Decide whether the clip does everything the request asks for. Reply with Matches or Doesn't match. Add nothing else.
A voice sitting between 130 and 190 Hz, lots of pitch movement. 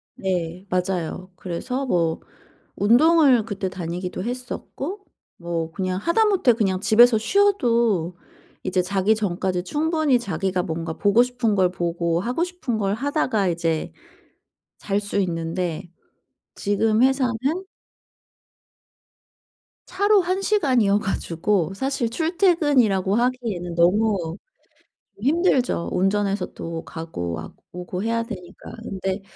Doesn't match